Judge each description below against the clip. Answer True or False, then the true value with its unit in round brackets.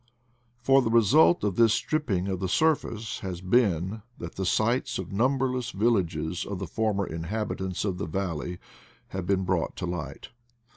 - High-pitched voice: False (95 Hz)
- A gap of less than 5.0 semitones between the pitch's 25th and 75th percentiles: True (4.5 semitones)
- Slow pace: False (165 wpm)